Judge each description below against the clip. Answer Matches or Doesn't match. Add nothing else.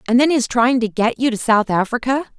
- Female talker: Matches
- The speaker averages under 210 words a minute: Doesn't match